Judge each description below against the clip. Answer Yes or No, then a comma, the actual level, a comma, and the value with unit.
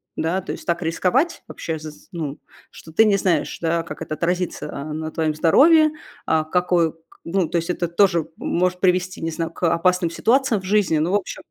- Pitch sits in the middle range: Yes, medium, 170 Hz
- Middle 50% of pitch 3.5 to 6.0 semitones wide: No, narrow, 2.5 semitones